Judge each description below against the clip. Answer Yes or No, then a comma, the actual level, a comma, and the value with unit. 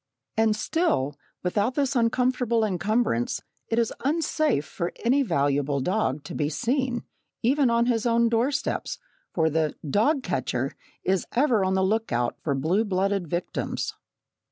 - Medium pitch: No, high, 215 Hz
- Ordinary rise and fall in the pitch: No, wide, 7.2 semitones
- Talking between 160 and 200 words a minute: No, average, 145 wpm